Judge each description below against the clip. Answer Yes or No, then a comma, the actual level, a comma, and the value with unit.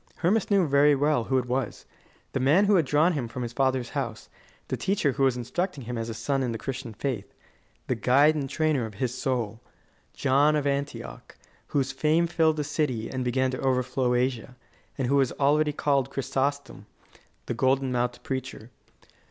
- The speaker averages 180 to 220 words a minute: Yes, average, 185 wpm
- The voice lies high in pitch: No, low, 135 Hz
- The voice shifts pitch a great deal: No, average, 2.9 semitones